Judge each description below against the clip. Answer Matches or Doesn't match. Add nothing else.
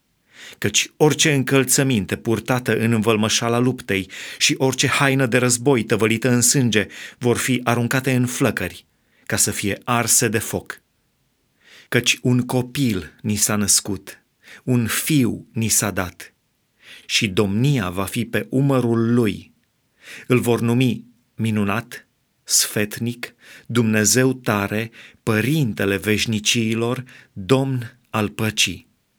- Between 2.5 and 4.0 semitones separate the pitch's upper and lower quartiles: Matches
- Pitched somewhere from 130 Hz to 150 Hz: Doesn't match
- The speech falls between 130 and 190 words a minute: Doesn't match